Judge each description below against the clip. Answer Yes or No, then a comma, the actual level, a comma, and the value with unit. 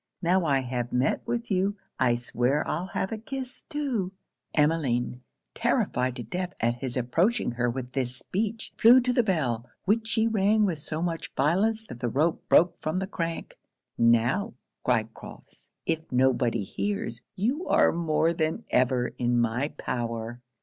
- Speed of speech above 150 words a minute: Yes, average, 165 wpm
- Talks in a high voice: No, medium, 155 Hz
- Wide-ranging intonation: Yes, wide, 8.5 semitones